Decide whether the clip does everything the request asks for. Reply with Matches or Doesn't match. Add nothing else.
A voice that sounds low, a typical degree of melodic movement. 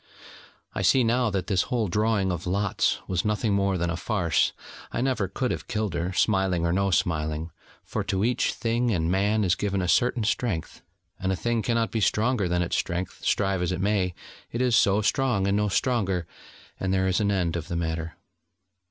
Matches